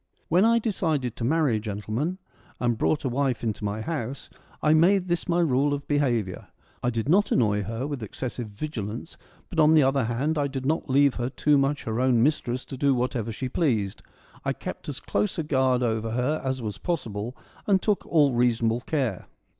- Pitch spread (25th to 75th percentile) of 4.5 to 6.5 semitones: Yes, average, 4.8 semitones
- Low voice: Yes, low, 130 Hz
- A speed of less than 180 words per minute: No, average, 195 wpm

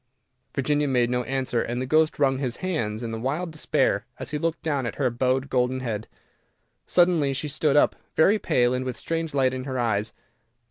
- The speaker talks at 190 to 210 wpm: Yes, average, 200 wpm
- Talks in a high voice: No, low, 130 Hz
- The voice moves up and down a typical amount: Yes, average, 3.5 semitones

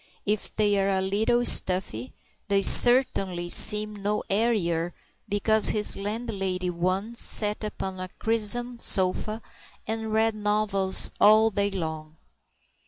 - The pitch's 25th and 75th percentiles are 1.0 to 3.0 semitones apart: Yes, narrow, 2.5 semitones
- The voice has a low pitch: No, high, 205 Hz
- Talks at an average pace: No, slow, 120 wpm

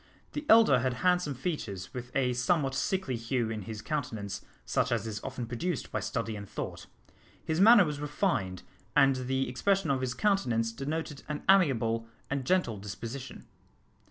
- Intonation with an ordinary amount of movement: No, wide, 5.7 semitones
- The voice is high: No, low, 130 Hz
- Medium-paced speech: Yes, average, 160 wpm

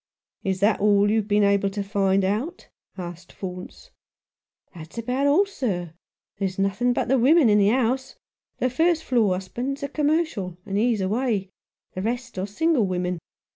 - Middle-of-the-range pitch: No, high, 210 Hz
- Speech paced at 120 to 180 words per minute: Yes, average, 175 wpm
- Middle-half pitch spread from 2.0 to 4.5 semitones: No, average, 5.1 semitones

